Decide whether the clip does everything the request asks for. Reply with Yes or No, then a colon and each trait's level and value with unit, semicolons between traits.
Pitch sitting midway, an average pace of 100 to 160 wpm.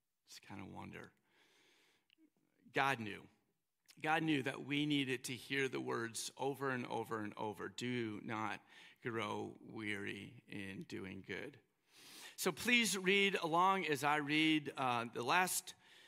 Yes: medium, 150 Hz; average, 140 wpm